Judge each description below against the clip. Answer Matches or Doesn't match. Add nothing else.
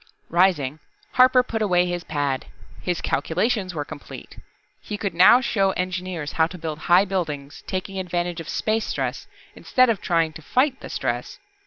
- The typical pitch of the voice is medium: Matches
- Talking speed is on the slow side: Doesn't match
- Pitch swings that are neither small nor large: Matches